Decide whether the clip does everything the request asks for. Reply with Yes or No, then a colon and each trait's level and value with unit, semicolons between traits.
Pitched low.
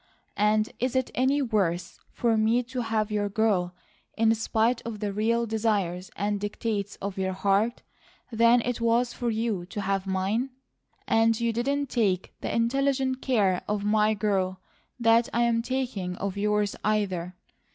No: high, 220 Hz